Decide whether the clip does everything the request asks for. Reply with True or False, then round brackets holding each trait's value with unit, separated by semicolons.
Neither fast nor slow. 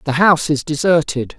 True (175 wpm)